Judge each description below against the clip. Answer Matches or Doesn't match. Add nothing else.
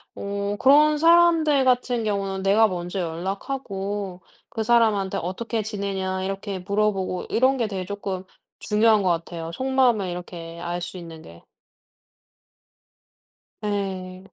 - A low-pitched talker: Doesn't match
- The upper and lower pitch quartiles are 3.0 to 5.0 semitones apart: Matches